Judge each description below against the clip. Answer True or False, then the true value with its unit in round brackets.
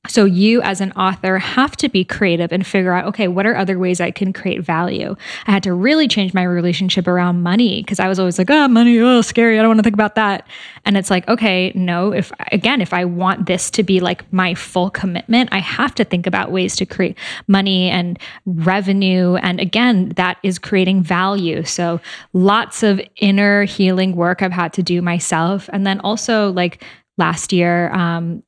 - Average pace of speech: False (210 wpm)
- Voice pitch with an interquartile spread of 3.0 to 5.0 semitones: False (2.4 semitones)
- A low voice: False (190 Hz)